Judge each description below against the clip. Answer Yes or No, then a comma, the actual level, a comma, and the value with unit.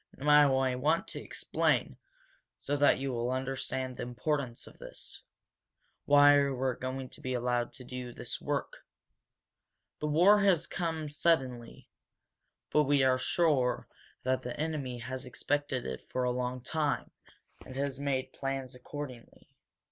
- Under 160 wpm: Yes, average, 150 wpm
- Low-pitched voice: Yes, low, 130 Hz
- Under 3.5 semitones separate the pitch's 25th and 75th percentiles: Yes, narrow, 2.4 semitones